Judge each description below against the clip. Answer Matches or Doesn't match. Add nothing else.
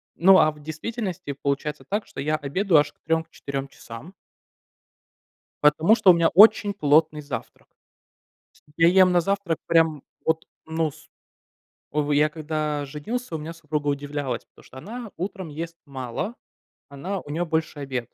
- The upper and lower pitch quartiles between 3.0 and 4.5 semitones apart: Matches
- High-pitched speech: Doesn't match